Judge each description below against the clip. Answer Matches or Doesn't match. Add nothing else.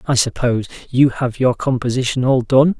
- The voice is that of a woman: Doesn't match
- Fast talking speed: Doesn't match